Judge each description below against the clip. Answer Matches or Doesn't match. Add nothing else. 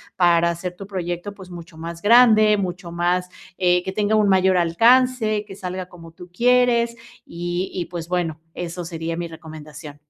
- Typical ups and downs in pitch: Matches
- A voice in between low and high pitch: Matches